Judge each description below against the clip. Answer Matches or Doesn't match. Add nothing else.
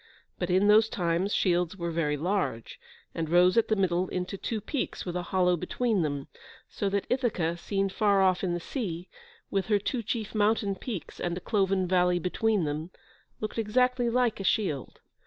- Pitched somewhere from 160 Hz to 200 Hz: Matches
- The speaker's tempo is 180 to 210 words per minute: Matches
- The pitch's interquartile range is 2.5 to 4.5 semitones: Matches